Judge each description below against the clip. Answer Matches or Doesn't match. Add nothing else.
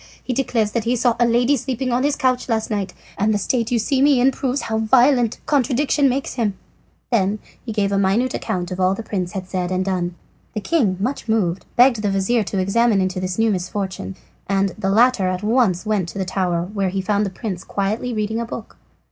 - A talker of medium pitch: Doesn't match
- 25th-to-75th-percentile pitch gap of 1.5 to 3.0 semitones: Doesn't match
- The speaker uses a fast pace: Matches